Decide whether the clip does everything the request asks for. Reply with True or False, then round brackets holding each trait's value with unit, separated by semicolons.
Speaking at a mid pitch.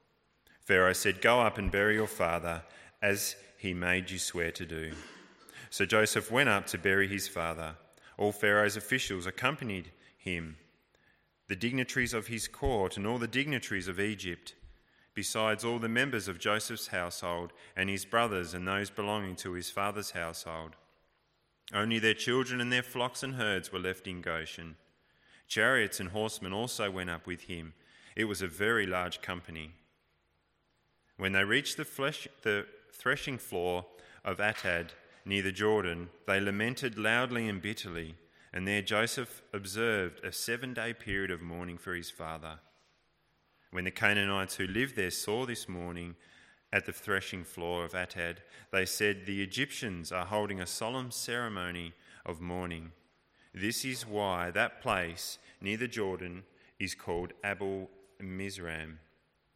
False (95 Hz)